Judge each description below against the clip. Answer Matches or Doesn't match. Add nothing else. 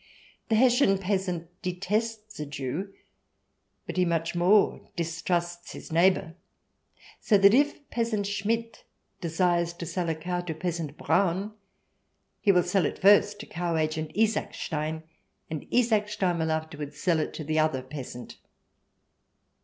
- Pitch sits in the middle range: Matches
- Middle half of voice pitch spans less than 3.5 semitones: Doesn't match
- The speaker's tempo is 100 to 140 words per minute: Matches